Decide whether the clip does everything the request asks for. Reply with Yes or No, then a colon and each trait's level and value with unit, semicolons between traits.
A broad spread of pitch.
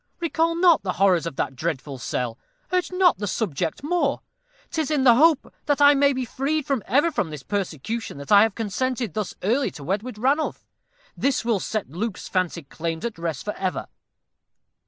Yes: wide, 8.6 semitones